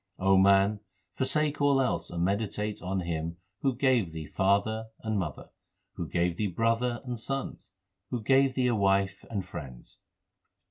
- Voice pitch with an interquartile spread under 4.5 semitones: No, average, 5.1 semitones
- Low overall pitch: Yes, low, 105 Hz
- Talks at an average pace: Yes, average, 155 wpm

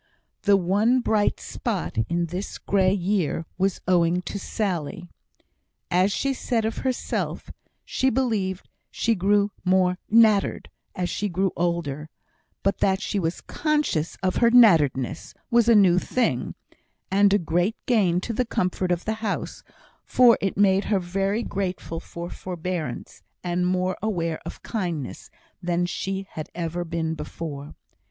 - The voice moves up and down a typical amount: Yes, average, 3.2 semitones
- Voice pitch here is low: No, medium, 185 Hz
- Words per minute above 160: No, average, 145 wpm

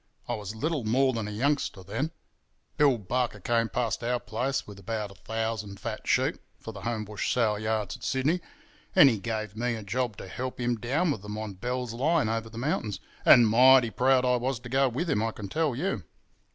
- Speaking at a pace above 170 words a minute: Yes, fast, 205 wpm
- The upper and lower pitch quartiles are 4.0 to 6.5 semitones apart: No, average, 3.3 semitones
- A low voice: Yes, low, 115 Hz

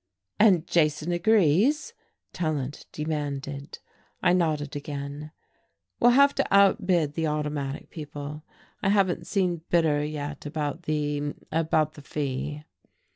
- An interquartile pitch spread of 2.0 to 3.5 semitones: Yes, average, 3.1 semitones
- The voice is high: No, medium, 155 Hz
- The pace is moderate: No, slow, 115 wpm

